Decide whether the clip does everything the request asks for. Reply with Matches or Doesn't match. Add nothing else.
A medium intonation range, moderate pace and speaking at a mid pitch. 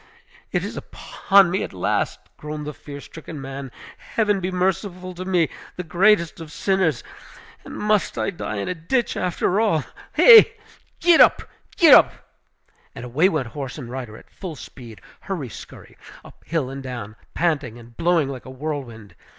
Doesn't match